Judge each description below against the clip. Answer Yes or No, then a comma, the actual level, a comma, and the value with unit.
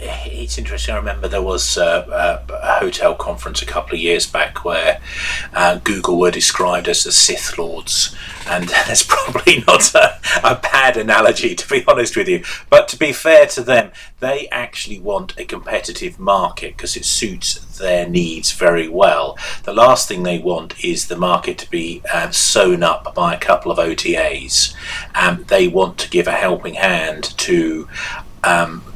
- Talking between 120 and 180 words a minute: Yes, average, 175 wpm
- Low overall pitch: No, very high, 310 Hz